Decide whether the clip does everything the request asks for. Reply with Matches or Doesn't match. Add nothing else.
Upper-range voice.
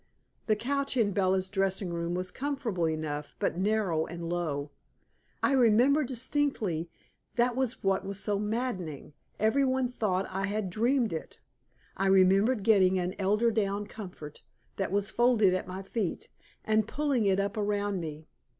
Matches